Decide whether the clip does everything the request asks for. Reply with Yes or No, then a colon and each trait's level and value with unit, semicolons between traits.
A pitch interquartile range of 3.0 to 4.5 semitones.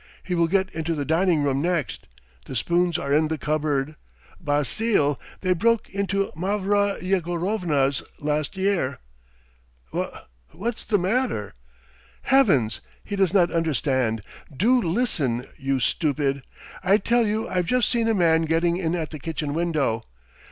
No: average, 5.2 semitones